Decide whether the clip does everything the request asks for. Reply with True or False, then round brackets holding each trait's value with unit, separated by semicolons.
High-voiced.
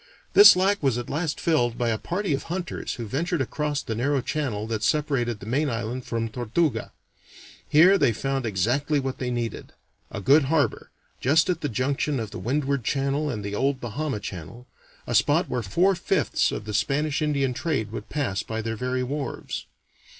False (135 Hz)